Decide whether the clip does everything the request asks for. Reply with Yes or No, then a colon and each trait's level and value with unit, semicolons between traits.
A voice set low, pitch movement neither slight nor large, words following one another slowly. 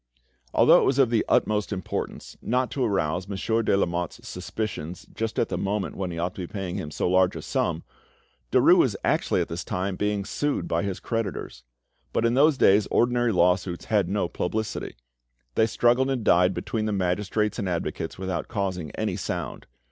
No: low, 100 Hz; average, 3.8 semitones; average, 185 wpm